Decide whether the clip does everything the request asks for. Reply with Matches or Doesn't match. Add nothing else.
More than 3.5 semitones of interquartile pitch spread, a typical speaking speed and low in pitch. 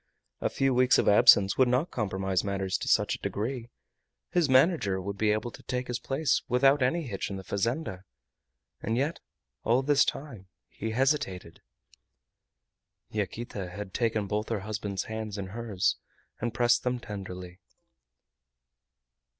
Matches